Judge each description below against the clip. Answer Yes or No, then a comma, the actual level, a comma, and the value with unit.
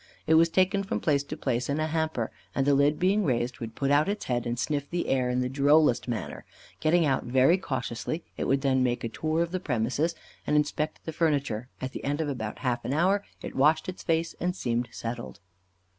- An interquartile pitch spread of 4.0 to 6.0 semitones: Yes, average, 4.4 semitones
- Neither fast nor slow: No, fast, 225 wpm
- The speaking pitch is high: No, medium, 145 Hz